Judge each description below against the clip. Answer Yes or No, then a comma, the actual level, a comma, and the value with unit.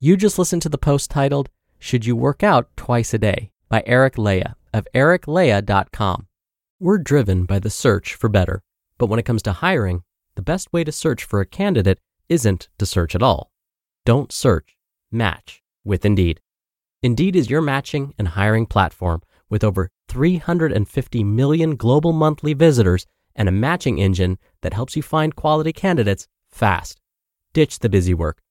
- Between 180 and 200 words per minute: No, average, 165 wpm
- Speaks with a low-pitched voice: Yes, low, 115 Hz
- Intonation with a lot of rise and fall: Yes, wide, 7.7 semitones